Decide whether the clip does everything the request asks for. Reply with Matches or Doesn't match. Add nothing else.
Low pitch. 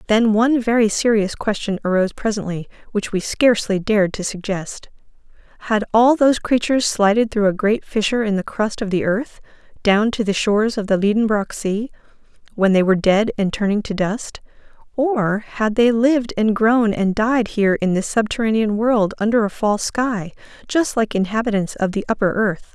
Doesn't match